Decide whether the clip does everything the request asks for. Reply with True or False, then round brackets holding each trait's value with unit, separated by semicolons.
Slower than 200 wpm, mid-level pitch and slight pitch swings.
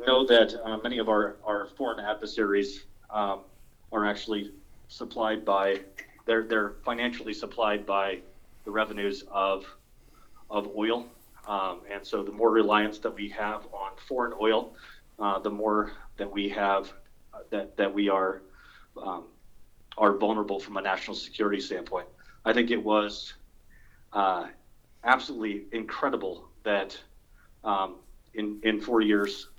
False (140 wpm; 105 Hz; 1.7 semitones)